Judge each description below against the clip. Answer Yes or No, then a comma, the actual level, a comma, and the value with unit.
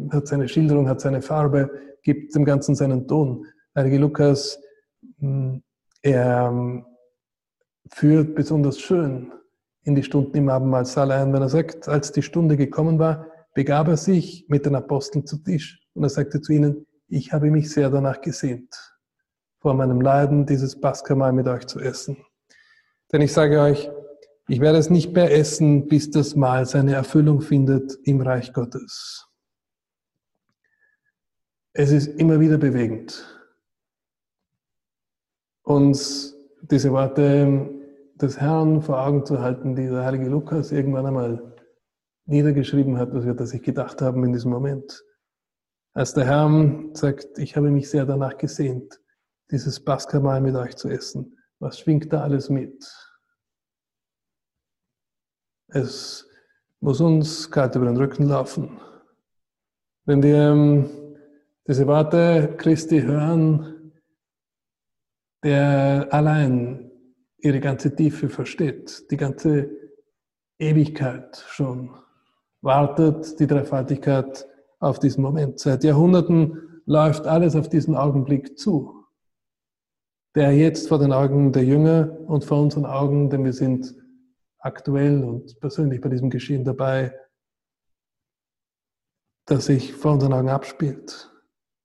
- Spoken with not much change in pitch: Yes, narrow, 2.2 semitones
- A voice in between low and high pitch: Yes, medium, 145 Hz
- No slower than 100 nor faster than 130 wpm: Yes, slow, 125 wpm